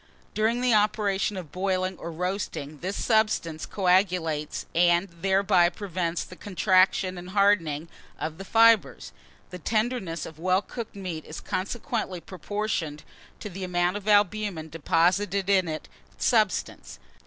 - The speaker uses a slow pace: Yes, slow, 130 wpm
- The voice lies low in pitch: No, medium, 185 Hz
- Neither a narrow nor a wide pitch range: Yes, average, 3.4 semitones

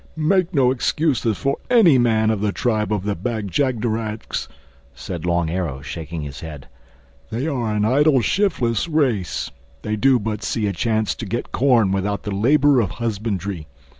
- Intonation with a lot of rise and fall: No, average, 4.9 semitones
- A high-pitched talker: No, low, 110 Hz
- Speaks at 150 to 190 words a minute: Yes, average, 165 wpm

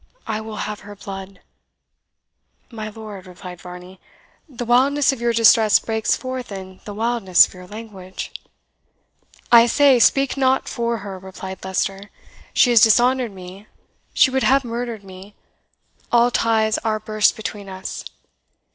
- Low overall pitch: No, high, 215 Hz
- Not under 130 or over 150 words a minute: Yes, average, 145 wpm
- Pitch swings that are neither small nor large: Yes, average, 3.7 semitones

